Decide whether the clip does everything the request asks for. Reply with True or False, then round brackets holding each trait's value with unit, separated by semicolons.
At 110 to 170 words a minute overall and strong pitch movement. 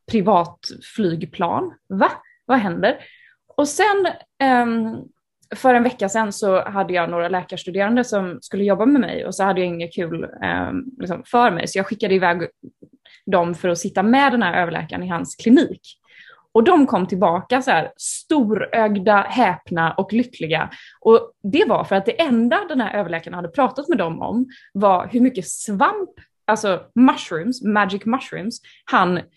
True (160 wpm; 5.7 semitones)